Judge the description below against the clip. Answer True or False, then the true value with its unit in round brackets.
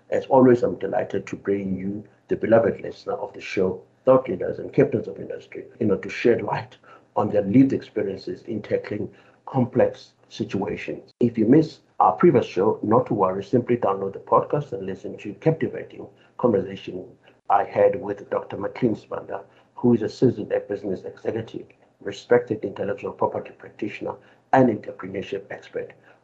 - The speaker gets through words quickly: False (160 wpm)